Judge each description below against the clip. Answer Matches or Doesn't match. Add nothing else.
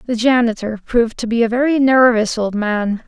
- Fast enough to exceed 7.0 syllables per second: Doesn't match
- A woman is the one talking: Matches